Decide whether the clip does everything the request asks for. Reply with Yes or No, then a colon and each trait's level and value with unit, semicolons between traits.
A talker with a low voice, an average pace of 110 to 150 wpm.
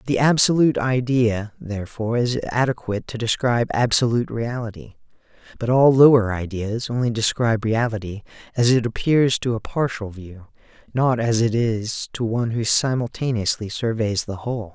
Yes: low, 115 Hz; average, 140 wpm